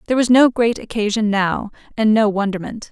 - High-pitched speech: Yes, high, 220 Hz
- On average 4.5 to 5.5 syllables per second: No, 5.7 syllables/s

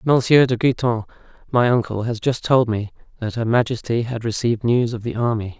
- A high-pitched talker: No, low, 115 Hz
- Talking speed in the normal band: Yes, average, 195 wpm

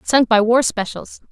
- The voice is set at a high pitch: Yes, high, 230 Hz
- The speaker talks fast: No, average, 180 wpm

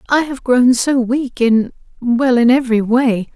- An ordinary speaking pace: Yes, average, 160 wpm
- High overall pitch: Yes, high, 245 Hz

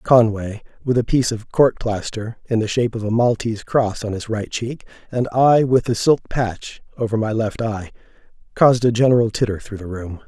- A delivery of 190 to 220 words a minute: Yes, fast, 205 wpm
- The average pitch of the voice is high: No, low, 115 Hz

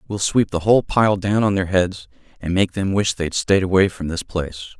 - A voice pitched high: No, very low, 95 Hz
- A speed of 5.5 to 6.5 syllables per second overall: No, 5.3 syllables/s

